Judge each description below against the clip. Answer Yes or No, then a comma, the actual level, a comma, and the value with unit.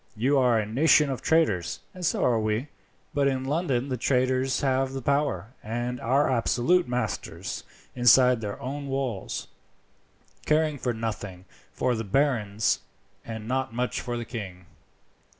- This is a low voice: Yes, low, 125 Hz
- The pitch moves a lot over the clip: No, average, 3.5 semitones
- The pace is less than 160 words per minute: Yes, average, 145 wpm